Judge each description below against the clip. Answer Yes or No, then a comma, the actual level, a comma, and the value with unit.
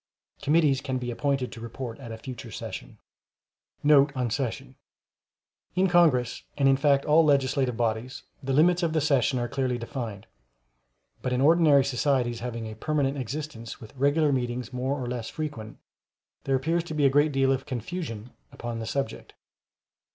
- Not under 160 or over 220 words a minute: Yes, average, 165 wpm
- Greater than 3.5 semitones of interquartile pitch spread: No, average, 3.2 semitones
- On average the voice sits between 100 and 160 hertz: Yes, low, 135 Hz